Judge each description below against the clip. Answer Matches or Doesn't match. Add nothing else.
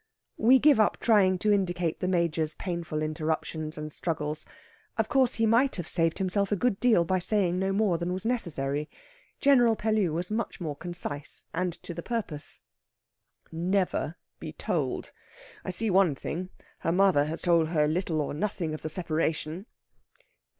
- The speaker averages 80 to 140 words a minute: Doesn't match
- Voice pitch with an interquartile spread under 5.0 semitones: Matches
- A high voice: Doesn't match